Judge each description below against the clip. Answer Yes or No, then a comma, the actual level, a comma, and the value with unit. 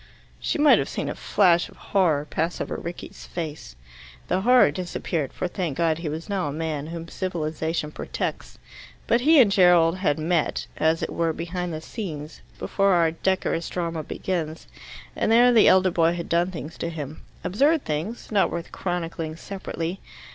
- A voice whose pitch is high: No, medium, 170 Hz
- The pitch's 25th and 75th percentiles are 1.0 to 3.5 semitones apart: Yes, average, 2.9 semitones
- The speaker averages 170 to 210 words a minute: Yes, average, 175 wpm